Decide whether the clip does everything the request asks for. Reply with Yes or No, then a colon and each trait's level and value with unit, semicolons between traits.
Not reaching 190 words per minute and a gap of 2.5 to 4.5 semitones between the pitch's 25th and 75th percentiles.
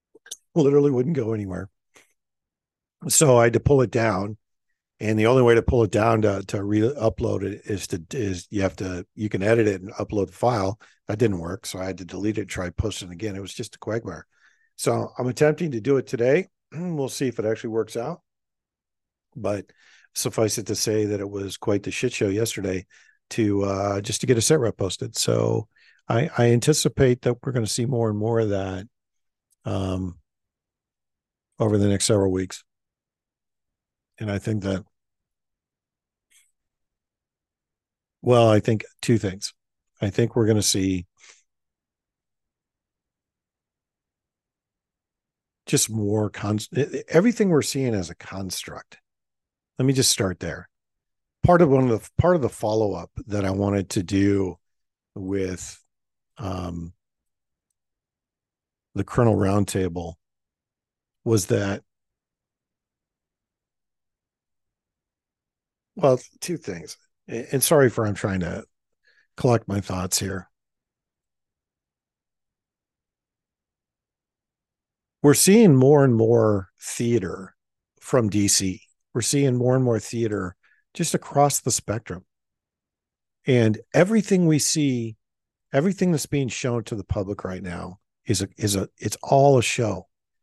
Yes: average, 140 wpm; average, 4.2 semitones